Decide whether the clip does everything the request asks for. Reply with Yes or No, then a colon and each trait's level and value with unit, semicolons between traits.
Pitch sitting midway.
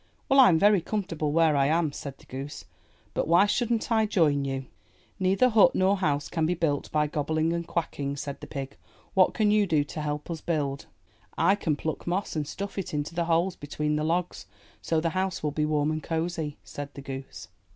Yes: medium, 160 Hz